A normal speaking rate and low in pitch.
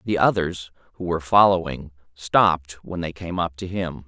Yes: average, 175 wpm; very low, 85 Hz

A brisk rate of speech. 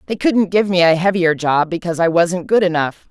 Yes: fast, 230 wpm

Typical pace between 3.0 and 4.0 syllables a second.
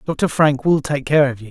No: 5.0 syllables/s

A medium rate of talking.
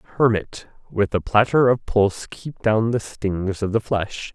Yes: average, 180 wpm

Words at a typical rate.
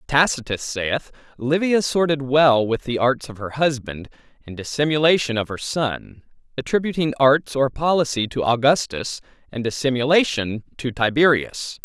No: slow, 130 wpm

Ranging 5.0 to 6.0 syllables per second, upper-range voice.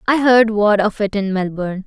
Yes: 5.2 syllables/s; high, 210 Hz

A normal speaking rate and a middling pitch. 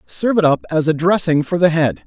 No: fast, 260 wpm; medium, 155 Hz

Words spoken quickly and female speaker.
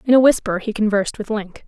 Yes: fast, 250 wpm; female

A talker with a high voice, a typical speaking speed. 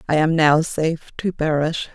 No: medium, 155 Hz; average, 185 wpm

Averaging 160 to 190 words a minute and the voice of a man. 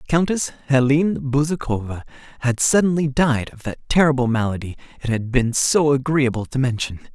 No: average, 145 wpm; male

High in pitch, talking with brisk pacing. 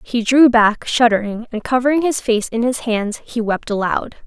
No: high, 235 Hz; average, 195 wpm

